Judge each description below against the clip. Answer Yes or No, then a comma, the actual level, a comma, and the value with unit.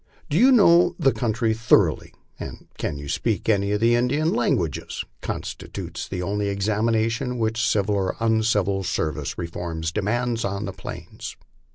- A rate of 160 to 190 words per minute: No, average, 145 wpm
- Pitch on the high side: No, low, 110 Hz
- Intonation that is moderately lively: Yes, average, 3.4 semitones